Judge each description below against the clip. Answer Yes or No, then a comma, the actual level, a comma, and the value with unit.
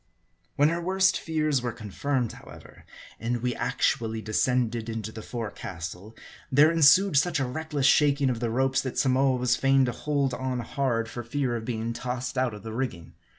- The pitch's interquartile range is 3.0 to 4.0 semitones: Yes, average, 3.6 semitones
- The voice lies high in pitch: No, low, 125 Hz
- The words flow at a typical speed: Yes, average, 180 wpm